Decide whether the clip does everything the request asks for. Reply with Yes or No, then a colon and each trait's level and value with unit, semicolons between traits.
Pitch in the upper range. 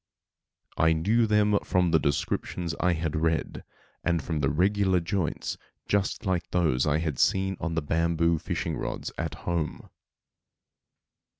No: very low, 85 Hz